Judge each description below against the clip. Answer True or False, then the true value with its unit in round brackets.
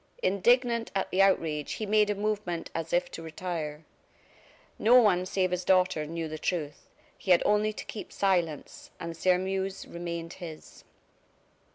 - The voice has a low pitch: False (180 Hz)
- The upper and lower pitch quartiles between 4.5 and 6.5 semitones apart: False (3.3 semitones)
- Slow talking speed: False (155 wpm)